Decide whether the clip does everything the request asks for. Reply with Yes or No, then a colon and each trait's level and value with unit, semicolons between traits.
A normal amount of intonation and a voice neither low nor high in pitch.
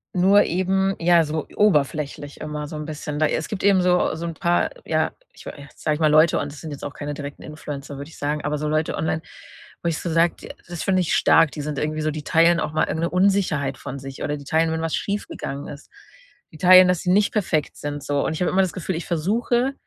Yes: average, 3.4 semitones; medium, 160 Hz